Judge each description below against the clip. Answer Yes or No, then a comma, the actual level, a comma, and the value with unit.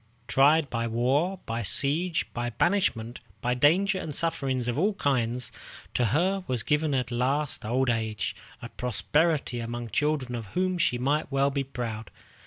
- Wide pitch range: No, average, 4.3 semitones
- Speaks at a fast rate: No, average, 165 wpm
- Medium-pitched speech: No, low, 130 Hz